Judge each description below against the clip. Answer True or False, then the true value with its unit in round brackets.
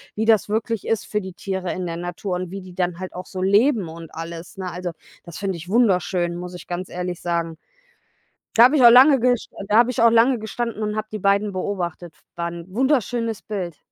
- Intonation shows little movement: False (4.1 semitones)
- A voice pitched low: False (190 Hz)